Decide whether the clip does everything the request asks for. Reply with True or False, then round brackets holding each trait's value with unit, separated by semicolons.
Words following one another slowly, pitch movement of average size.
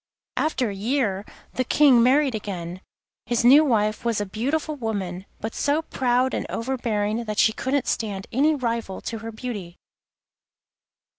False (150 wpm; 4.0 semitones)